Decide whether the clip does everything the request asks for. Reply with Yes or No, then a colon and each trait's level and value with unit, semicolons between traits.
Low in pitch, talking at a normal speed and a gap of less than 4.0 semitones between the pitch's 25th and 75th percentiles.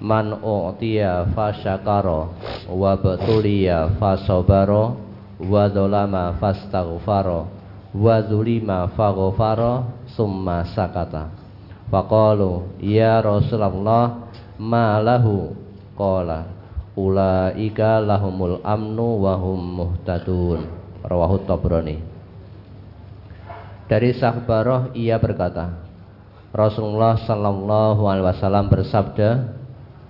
No: low, 100 Hz; slow, 70 wpm; narrow, 2.6 semitones